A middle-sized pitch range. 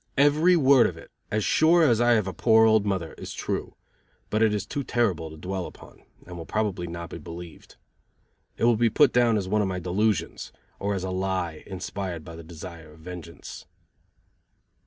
Yes: average, 4.6 semitones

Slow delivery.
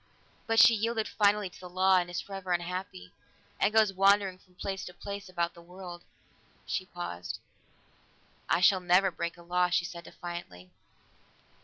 No: average, 165 wpm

